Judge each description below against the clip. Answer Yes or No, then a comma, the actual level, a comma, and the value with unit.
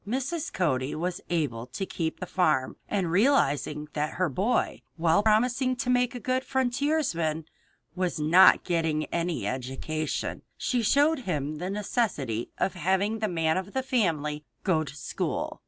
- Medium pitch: Yes, medium, 180 Hz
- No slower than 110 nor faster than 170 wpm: Yes, average, 155 wpm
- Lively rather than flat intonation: Yes, wide, 7.3 semitones